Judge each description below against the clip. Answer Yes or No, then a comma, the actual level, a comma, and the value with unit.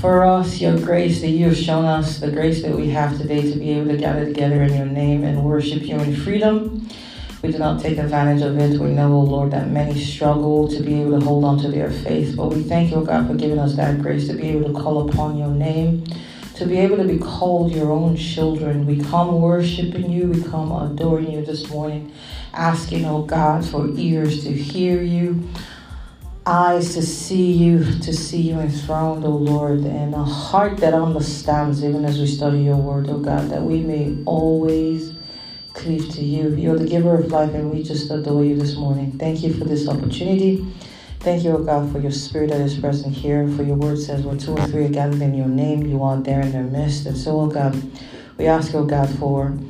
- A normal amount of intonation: No, narrow, 1.9 semitones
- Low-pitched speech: No, medium, 150 Hz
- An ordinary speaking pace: No, fast, 220 wpm